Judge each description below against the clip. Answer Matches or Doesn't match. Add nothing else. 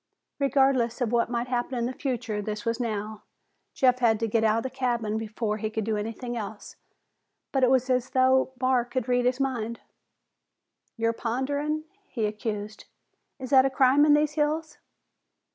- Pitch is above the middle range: Matches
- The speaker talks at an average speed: Matches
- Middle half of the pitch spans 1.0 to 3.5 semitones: Matches